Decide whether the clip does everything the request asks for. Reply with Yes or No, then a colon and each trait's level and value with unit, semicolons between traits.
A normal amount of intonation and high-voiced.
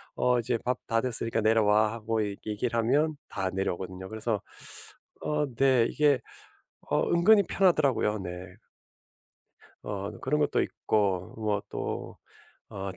No: average, 4.2 semitones; low, 110 Hz